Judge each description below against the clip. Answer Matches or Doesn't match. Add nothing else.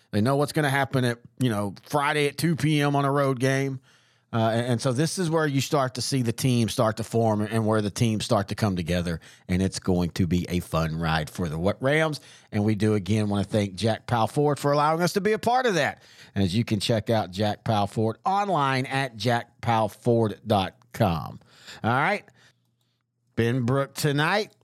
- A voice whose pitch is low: Matches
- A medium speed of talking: Doesn't match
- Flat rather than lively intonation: Doesn't match